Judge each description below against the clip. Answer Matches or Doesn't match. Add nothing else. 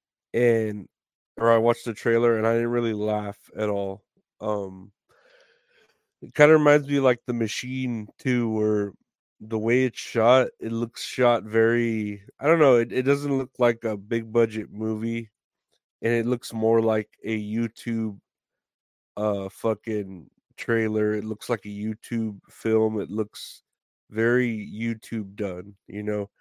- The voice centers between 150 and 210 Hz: Doesn't match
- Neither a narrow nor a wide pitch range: Doesn't match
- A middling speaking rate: Matches